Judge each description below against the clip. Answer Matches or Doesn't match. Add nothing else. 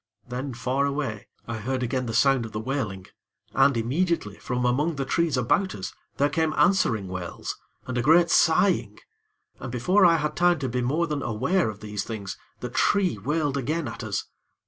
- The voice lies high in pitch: Doesn't match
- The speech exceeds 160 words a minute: Matches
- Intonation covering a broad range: Matches